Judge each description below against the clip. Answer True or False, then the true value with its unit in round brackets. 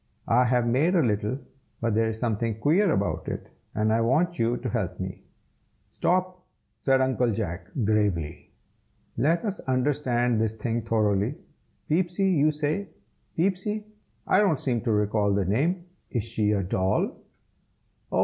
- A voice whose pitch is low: True (120 Hz)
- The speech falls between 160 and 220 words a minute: False (150 wpm)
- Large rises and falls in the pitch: True (6.4 semitones)